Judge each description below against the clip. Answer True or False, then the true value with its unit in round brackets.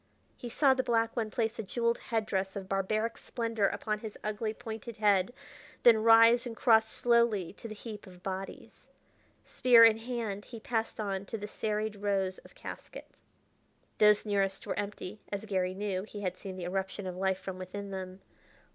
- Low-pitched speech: False (210 Hz)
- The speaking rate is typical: True (180 wpm)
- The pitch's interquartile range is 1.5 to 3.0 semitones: True (2.7 semitones)